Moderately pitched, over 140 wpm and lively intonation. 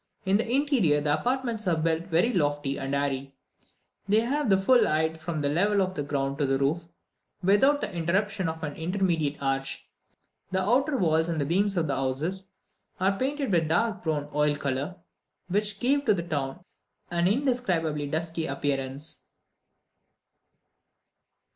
Yes: medium, 170 Hz; average, 160 wpm; wide, 5.8 semitones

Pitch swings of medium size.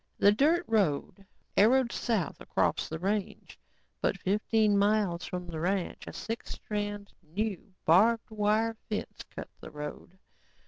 Yes: average, 3.3 semitones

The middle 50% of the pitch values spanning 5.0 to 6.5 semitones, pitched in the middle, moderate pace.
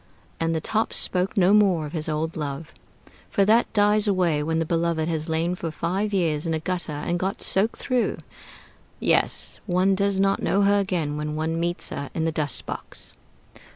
No: average, 3.7 semitones; medium, 170 Hz; average, 190 wpm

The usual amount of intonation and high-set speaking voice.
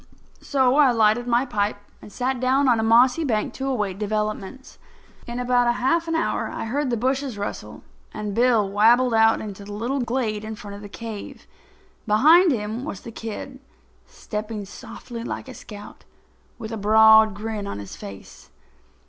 Yes: average, 3.3 semitones; high, 225 Hz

